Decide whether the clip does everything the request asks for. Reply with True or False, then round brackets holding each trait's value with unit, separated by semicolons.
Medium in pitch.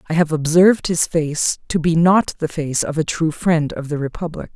True (160 Hz)